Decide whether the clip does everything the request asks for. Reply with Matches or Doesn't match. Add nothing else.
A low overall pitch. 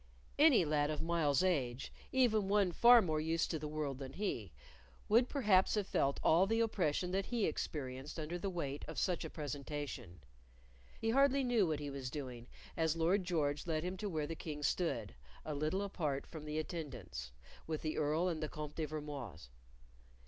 Doesn't match